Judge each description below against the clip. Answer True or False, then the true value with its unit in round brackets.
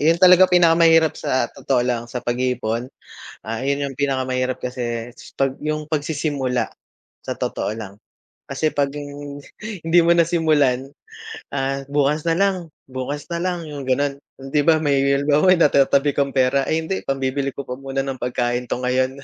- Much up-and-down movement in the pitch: False (3.3 semitones)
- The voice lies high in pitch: False (140 Hz)